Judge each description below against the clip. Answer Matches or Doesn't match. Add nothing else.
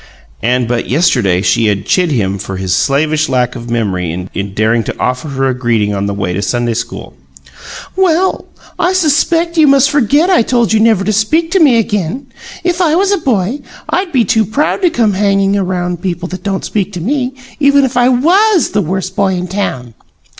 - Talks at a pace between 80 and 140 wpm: Doesn't match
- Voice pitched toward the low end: Doesn't match